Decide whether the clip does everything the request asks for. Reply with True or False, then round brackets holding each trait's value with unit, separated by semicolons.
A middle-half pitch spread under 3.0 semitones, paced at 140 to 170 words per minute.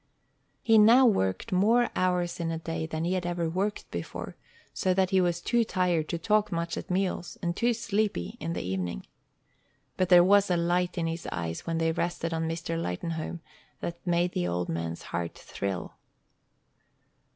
False (2.5 semitones; 180 wpm)